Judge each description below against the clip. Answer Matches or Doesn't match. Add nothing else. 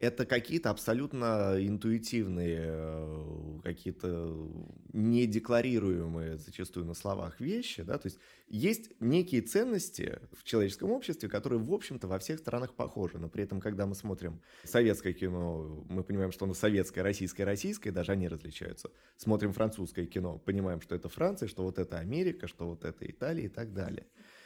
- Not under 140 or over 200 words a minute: Matches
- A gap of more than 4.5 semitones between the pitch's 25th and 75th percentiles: Matches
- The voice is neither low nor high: Doesn't match